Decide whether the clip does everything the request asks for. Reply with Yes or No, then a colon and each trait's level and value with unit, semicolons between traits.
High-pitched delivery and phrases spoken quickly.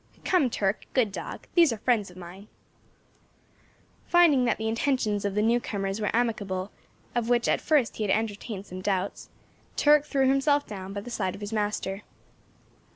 No: high, 215 Hz; average, 175 wpm